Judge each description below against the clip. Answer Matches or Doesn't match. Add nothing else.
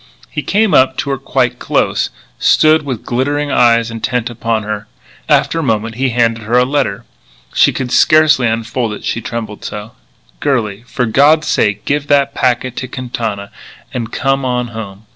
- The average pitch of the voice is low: Matches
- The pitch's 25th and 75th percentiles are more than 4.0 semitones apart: Doesn't match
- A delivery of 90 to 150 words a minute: Doesn't match